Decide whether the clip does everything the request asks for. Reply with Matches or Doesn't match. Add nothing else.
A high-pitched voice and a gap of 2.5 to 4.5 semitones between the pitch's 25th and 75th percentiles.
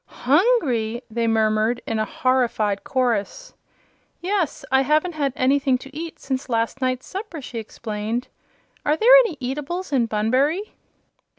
Doesn't match